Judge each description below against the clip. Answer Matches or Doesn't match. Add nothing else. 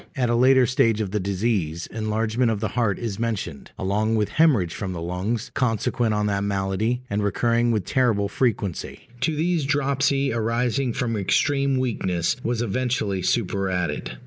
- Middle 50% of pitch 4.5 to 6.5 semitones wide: Doesn't match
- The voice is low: Matches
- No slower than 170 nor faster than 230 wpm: Doesn't match